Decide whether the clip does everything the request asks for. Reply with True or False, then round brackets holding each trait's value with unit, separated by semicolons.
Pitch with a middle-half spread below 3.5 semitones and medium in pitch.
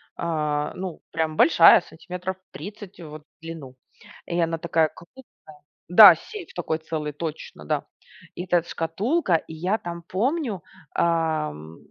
True (2.6 semitones; 165 Hz)